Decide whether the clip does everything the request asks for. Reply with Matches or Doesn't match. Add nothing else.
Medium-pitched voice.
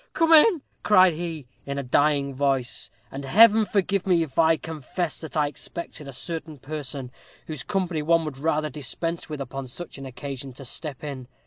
Matches